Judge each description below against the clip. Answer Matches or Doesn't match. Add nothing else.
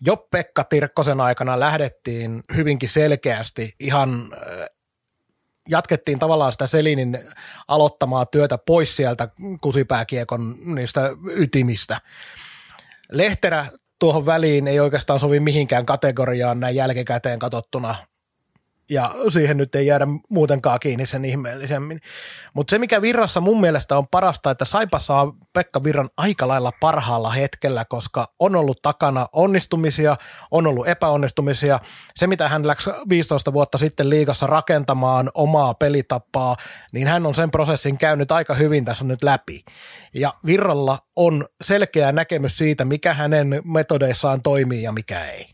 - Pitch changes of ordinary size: Matches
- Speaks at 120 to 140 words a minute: Matches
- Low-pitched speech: Doesn't match